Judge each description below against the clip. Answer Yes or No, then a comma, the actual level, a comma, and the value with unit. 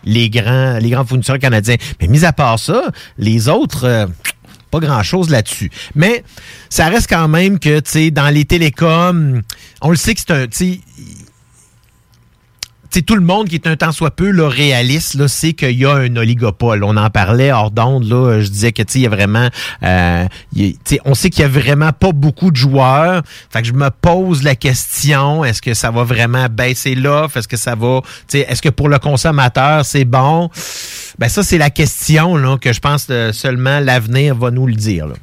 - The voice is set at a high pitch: No, low, 135 Hz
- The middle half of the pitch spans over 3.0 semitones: Yes, average, 4.5 semitones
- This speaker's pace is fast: No, average, 210 wpm